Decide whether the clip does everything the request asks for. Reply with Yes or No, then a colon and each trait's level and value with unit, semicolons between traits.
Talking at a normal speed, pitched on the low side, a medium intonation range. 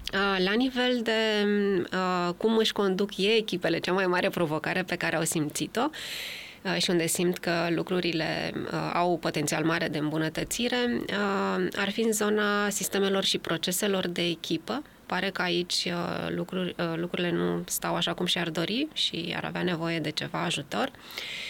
No: average, 165 wpm; medium, 180 Hz; average, 3.3 semitones